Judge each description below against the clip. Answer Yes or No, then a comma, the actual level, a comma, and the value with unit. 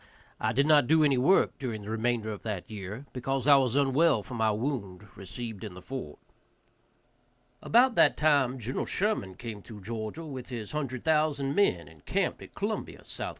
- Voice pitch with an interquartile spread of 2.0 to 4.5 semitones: No, average, 4.9 semitones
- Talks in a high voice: No, low, 125 Hz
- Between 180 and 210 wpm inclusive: Yes, average, 185 wpm